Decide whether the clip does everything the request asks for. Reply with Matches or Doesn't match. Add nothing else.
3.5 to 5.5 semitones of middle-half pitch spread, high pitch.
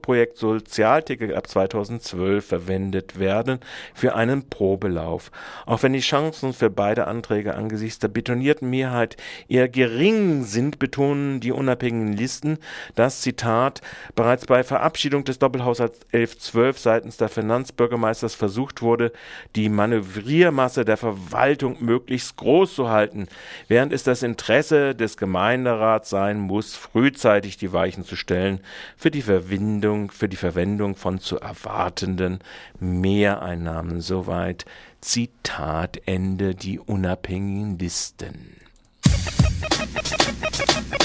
Doesn't match